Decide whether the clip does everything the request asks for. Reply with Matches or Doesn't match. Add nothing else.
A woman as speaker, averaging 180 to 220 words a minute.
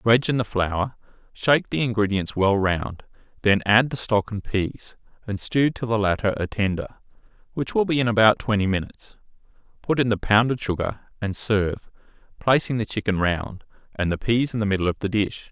Doesn't match